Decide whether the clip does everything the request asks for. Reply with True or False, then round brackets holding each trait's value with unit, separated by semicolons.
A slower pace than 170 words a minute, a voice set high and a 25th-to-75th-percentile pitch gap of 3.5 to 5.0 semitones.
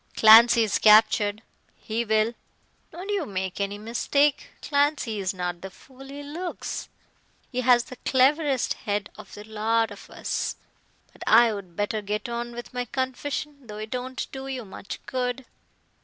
True (155 wpm; 235 Hz; 3.9 semitones)